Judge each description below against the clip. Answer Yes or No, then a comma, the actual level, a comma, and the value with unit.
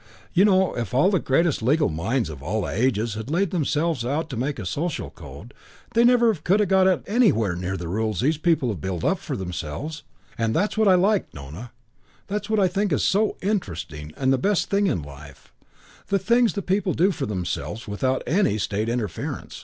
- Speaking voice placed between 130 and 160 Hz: Yes, low, 135 Hz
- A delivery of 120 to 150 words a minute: No, average, 200 wpm